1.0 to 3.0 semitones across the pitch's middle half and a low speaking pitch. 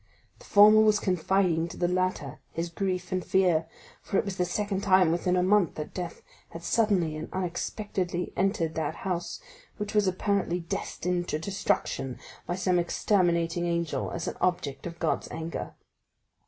No: narrow, 2.4 semitones; medium, 180 Hz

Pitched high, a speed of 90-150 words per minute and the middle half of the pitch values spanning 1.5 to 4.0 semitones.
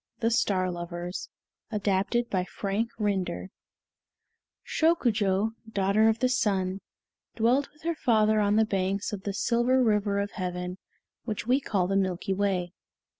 Yes: high, 205 Hz; average, 140 wpm; average, 3.2 semitones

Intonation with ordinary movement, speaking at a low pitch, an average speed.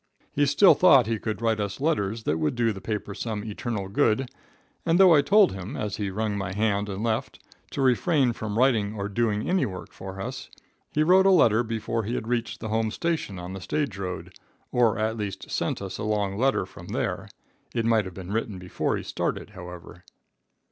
No: average, 3.5 semitones; low, 110 Hz; fast, 210 wpm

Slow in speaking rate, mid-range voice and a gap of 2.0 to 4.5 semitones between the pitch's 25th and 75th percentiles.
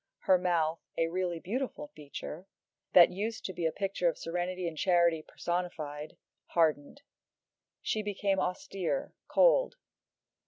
Yes: slow, 125 wpm; medium, 180 Hz; average, 3.1 semitones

